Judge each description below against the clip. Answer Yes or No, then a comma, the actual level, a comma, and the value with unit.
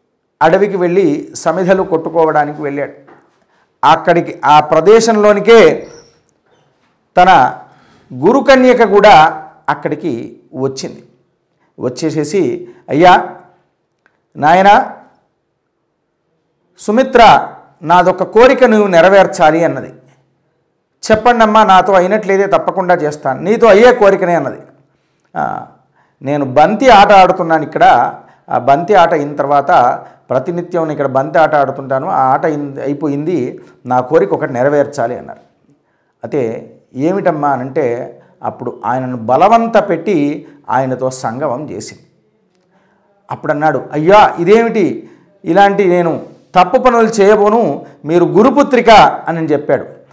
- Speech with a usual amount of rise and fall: No, wide, 6.0 semitones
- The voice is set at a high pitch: No, medium, 175 Hz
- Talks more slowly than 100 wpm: Yes, average, 90 wpm